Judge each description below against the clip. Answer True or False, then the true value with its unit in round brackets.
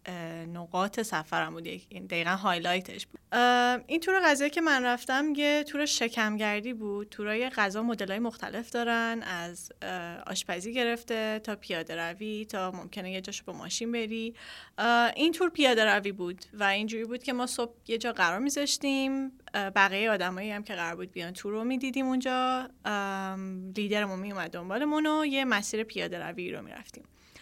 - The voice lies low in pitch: False (215 Hz)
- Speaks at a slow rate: False (155 wpm)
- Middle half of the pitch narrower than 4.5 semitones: False (4.8 semitones)